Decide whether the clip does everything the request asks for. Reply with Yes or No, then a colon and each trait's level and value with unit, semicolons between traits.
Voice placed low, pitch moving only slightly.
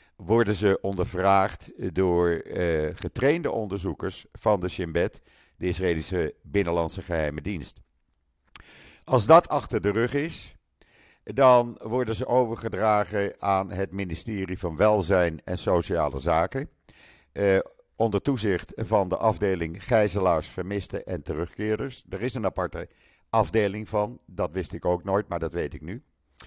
No: low, 100 Hz; average, 3.5 semitones